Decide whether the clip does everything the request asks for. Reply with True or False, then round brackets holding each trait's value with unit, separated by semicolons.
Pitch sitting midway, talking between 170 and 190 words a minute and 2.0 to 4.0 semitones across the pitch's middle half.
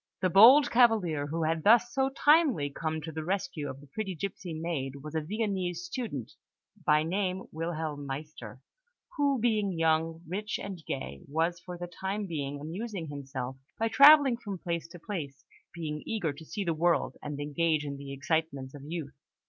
False (165 Hz; 175 wpm; 5.2 semitones)